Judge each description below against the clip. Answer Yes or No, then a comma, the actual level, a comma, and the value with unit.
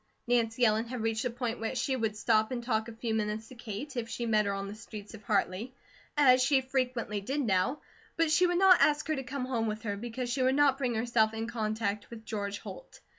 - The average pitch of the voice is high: Yes, high, 230 Hz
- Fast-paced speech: Yes, fast, 240 wpm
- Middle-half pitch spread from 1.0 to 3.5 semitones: Yes, average, 3.0 semitones